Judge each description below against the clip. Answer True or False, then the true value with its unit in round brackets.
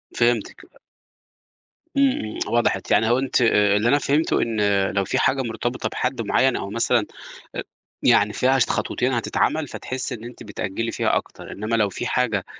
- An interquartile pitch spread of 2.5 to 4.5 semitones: True (3.2 semitones)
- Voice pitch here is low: True (120 Hz)